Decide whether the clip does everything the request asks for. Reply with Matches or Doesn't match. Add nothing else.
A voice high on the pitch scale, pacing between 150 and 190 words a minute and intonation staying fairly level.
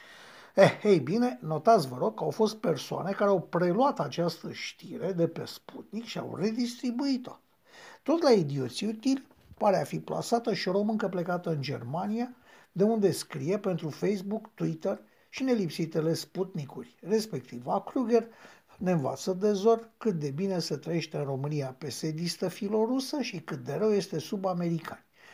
Doesn't match